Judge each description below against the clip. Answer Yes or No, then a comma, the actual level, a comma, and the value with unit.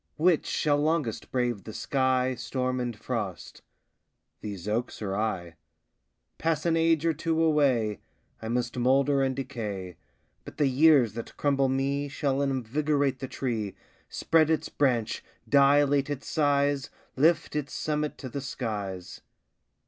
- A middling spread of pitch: Yes, average, 3.9 semitones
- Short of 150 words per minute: Yes, average, 140 wpm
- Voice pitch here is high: No, low, 135 Hz